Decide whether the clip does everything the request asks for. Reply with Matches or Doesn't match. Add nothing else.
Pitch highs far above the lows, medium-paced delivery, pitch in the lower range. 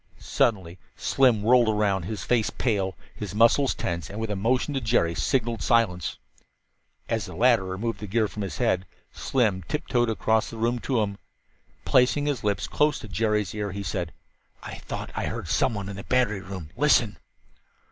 Doesn't match